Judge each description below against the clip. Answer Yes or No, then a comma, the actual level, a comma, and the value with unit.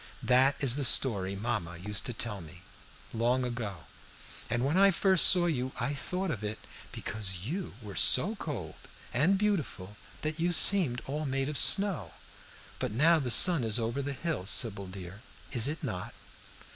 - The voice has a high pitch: No, low, 125 Hz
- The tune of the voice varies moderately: No, wide, 6.8 semitones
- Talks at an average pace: Yes, average, 170 wpm